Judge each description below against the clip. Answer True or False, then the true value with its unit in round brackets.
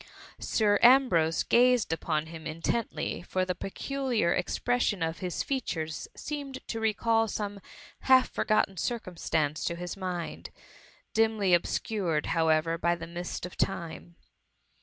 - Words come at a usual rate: False (130 wpm)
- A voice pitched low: False (185 Hz)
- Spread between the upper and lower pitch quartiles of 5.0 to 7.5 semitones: True (5.3 semitones)